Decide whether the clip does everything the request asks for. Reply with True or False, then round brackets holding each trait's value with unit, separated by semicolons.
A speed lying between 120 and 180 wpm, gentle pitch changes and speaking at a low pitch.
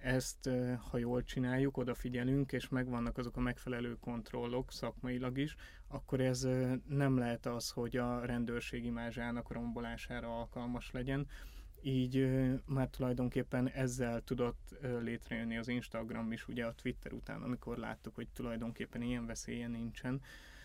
True (130 wpm; 1.5 semitones; 125 Hz)